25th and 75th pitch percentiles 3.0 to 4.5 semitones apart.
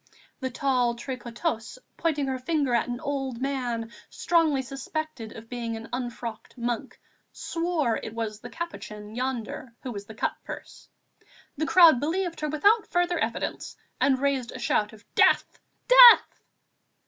No: average, 5.1 semitones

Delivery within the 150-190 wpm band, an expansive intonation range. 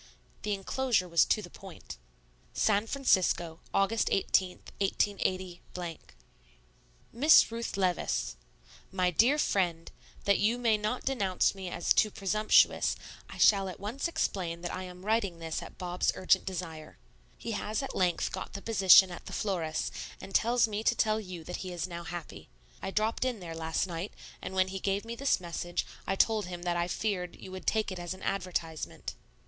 No: average, 175 wpm; average, 3.5 semitones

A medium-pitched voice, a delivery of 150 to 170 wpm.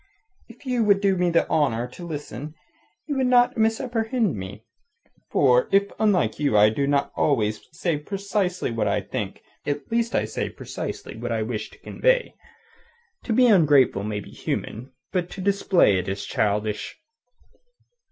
Yes: medium, 160 Hz; average, 160 wpm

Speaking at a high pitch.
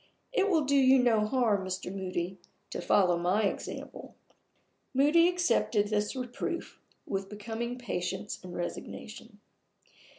Yes: high, 215 Hz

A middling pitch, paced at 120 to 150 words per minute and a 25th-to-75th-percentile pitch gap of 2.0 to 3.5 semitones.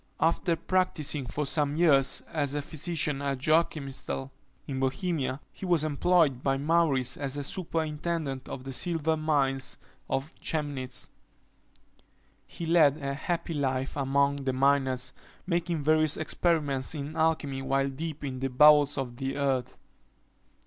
Yes: medium, 145 Hz; slow, 135 wpm; average, 2.9 semitones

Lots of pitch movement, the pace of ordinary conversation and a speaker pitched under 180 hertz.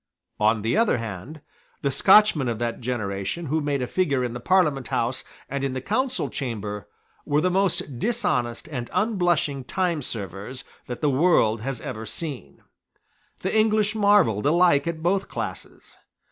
Yes: wide, 7.2 semitones; average, 155 wpm; medium, 140 Hz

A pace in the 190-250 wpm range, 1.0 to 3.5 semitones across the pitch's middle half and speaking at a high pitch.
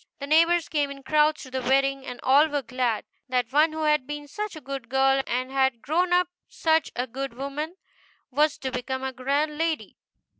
Yes: average, 200 wpm; average, 2.8 semitones; very high, 275 Hz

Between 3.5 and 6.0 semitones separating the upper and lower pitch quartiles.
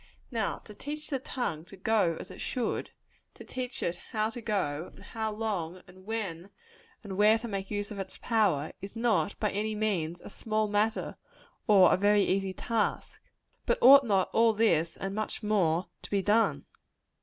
No: average, 3.0 semitones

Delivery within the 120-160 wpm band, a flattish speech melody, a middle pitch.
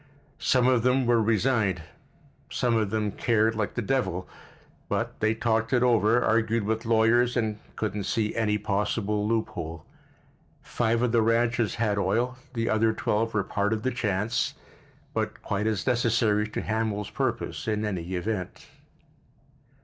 No: average, 150 wpm; narrow, 1.9 semitones; low, 110 Hz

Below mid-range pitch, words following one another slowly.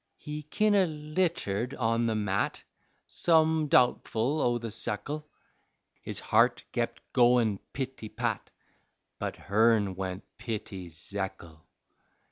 Yes: low, 115 Hz; slow, 110 wpm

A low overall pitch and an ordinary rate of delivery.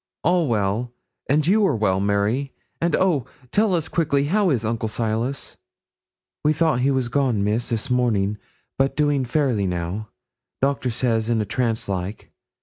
Yes: low, 125 Hz; average, 160 wpm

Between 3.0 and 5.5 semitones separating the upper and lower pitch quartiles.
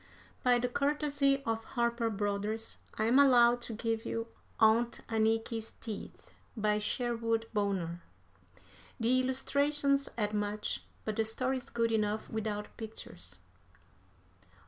No: narrow, 2.4 semitones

